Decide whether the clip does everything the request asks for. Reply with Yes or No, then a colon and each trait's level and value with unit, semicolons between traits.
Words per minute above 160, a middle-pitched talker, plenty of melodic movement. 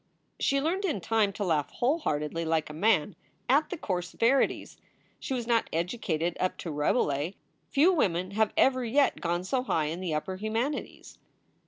No: average, 180 wpm; high, 200 Hz; wide, 7.5 semitones